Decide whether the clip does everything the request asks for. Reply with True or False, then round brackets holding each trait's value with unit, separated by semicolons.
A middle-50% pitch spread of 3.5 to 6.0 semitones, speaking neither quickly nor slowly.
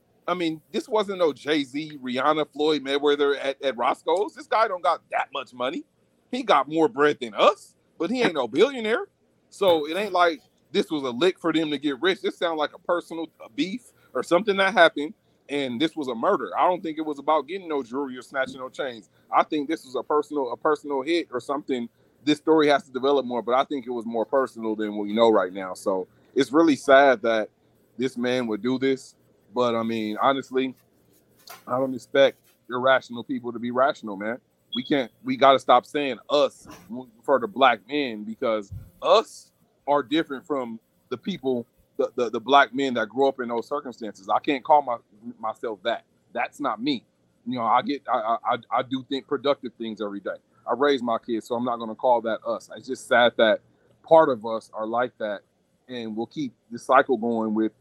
False (4.5 semitones; 210 wpm)